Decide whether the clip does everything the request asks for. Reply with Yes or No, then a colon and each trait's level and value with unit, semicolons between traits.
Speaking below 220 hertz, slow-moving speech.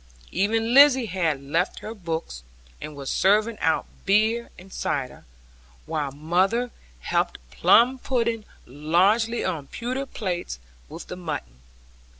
Yes: high, 190 Hz; slow, 125 wpm